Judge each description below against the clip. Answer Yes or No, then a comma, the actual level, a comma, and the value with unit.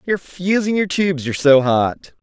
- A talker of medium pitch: Yes, medium, 165 Hz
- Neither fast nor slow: Yes, average, 190 wpm